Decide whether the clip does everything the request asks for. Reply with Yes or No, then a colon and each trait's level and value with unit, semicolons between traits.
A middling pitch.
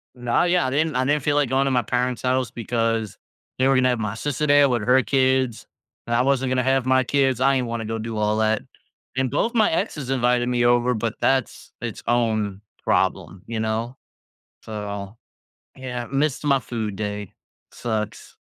No: low, 125 Hz